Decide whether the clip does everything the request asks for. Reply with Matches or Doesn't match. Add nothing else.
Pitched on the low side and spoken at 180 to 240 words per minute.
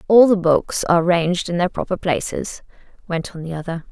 Doesn't match